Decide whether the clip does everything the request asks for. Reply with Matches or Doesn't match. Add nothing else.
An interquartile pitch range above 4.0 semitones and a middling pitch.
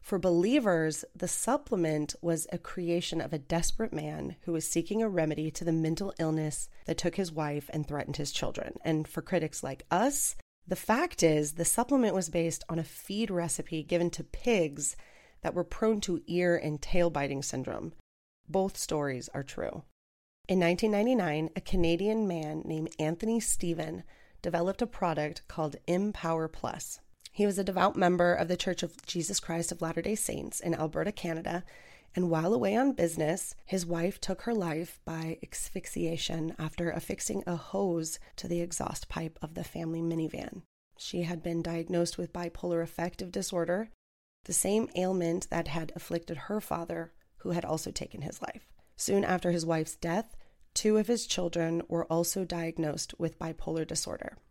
Doesn't match